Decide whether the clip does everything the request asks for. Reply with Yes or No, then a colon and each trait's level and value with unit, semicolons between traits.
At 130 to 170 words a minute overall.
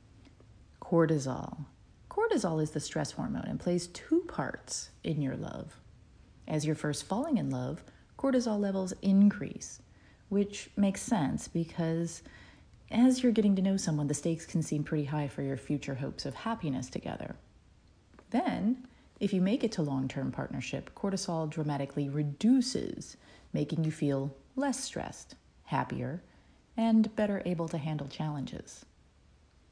Yes: average, 140 wpm